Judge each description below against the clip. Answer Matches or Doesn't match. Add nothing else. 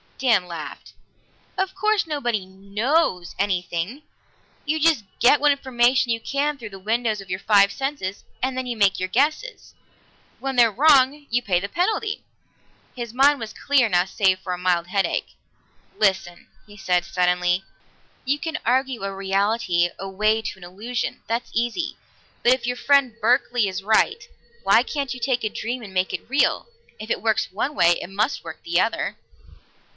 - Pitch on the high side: Matches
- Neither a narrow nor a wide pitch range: Doesn't match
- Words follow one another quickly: Doesn't match